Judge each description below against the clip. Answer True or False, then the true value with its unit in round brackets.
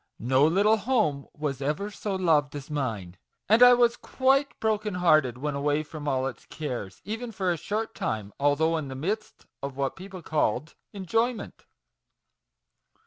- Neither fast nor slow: True (160 wpm)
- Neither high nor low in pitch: True (155 Hz)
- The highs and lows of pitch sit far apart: True (7.1 semitones)